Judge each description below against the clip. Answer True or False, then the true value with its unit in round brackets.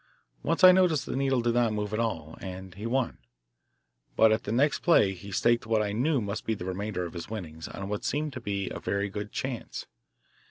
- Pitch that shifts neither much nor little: True (3.9 semitones)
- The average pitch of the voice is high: False (110 Hz)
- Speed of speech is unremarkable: False (210 wpm)